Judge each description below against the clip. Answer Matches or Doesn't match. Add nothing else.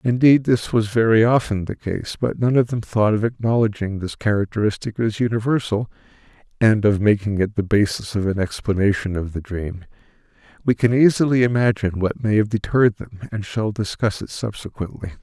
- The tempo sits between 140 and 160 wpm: Doesn't match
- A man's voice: Matches